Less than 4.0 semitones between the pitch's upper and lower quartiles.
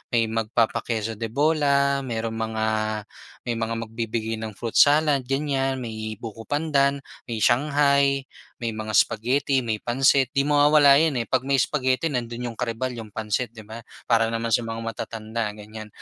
Yes: average, 3.6 semitones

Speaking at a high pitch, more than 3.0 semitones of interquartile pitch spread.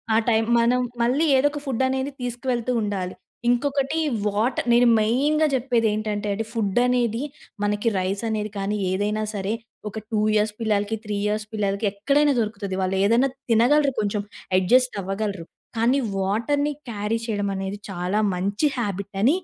Yes: high, 220 Hz; average, 3.5 semitones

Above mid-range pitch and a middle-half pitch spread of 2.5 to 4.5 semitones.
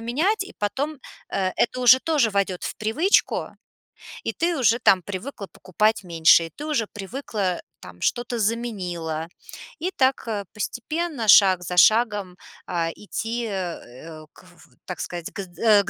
No: high, 210 Hz; wide, 5.4 semitones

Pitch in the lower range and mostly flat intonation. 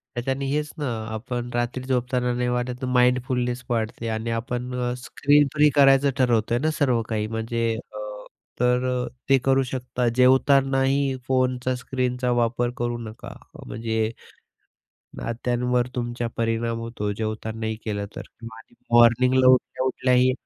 Yes: low, 125 Hz; narrow, 1.8 semitones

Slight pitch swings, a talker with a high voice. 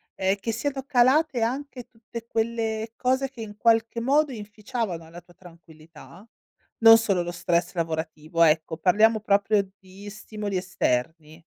No: average, 5.0 semitones; high, 210 Hz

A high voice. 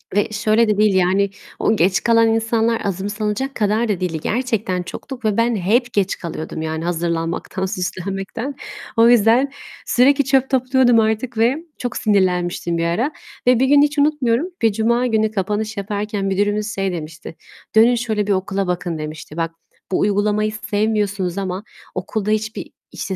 Yes: high, 210 Hz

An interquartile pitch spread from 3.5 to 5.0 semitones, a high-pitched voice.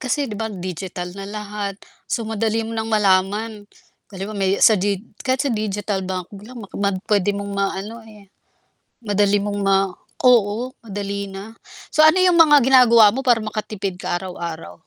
No: narrow, 2.5 semitones; high, 205 Hz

